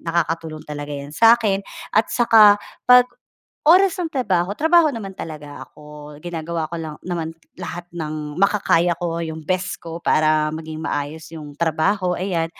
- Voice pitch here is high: No, medium, 170 Hz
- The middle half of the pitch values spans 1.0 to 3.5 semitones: No, average, 4.2 semitones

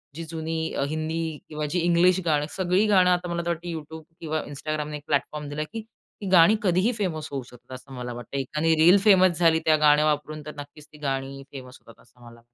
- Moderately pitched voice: Yes, medium, 155 Hz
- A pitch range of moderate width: Yes, average, 3.0 semitones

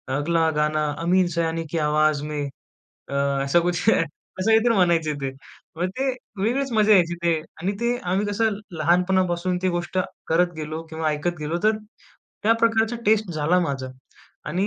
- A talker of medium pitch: Yes, medium, 175 Hz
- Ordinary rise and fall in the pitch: Yes, average, 4.6 semitones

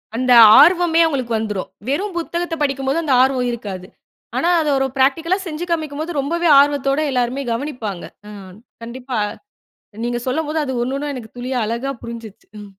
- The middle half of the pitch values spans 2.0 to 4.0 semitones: No, average, 4.5 semitones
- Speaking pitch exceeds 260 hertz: Yes, very high, 270 Hz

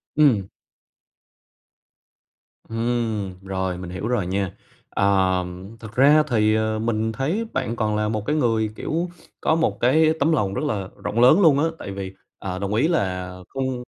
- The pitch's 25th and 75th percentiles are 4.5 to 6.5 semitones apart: Yes, wide, 5.5 semitones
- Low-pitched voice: Yes, low, 110 Hz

